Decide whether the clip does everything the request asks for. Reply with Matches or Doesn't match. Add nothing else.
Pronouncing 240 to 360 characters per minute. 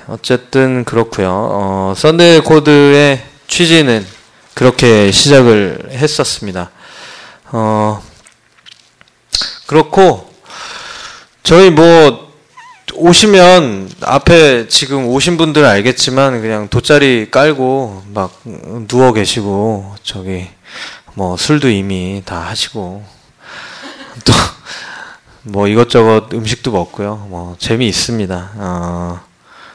Doesn't match